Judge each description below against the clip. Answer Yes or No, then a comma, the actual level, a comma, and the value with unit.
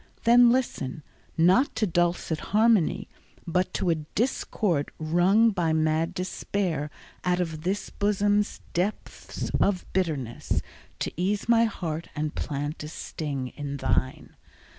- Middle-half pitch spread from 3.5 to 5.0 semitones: Yes, average, 4.7 semitones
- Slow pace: Yes, slow, 125 wpm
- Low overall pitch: No, medium, 175 Hz